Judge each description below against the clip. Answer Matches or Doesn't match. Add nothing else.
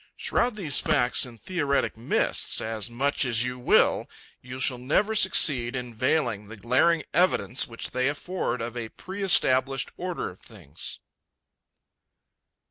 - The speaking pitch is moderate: Doesn't match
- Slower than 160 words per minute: Matches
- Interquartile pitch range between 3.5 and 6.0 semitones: Matches